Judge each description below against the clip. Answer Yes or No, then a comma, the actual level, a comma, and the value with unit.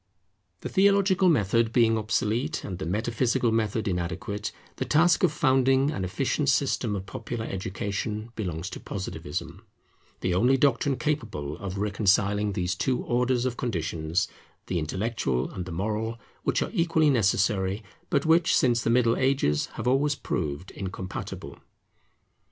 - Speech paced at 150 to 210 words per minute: No, average, 140 wpm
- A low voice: Yes, low, 110 Hz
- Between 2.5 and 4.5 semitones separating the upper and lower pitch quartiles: No, wide, 5.6 semitones